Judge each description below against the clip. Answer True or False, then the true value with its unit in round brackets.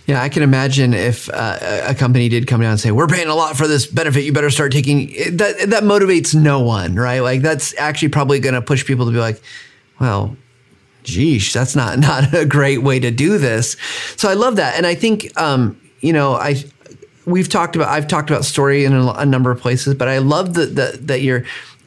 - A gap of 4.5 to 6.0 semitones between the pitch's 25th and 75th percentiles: False (3.3 semitones)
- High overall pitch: False (140 Hz)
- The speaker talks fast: True (230 wpm)